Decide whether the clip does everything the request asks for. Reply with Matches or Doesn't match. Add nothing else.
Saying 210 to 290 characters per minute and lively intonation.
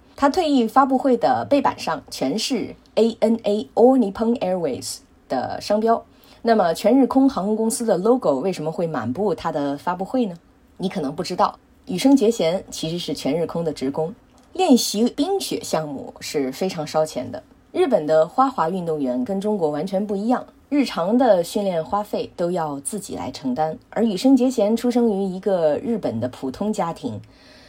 Doesn't match